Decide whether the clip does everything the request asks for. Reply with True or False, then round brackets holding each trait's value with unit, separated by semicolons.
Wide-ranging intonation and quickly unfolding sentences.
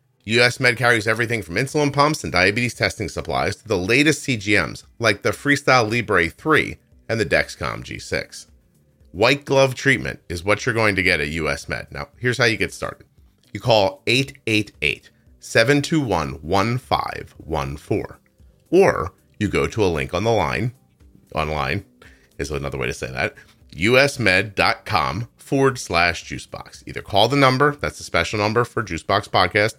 False (7.0 semitones; 155 wpm)